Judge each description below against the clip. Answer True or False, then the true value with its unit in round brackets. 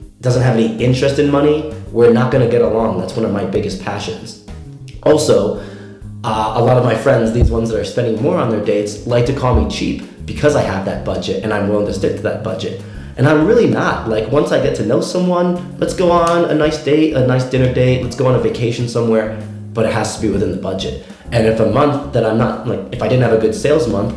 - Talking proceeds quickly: True (255 wpm)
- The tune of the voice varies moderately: True (3.5 semitones)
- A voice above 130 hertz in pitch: False (115 Hz)